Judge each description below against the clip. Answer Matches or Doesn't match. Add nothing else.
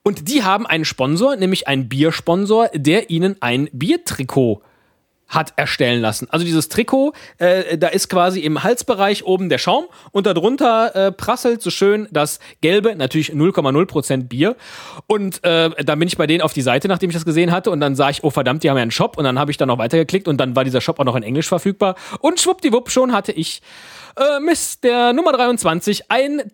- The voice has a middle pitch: Matches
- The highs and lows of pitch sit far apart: Matches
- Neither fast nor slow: Doesn't match